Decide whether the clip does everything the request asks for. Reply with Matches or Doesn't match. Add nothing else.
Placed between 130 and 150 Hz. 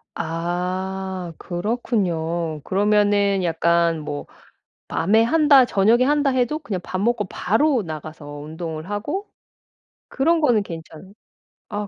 Doesn't match